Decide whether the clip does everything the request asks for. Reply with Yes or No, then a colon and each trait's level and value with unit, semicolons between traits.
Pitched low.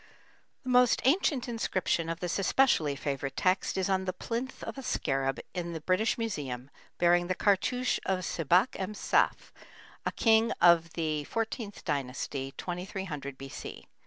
No: medium, 180 Hz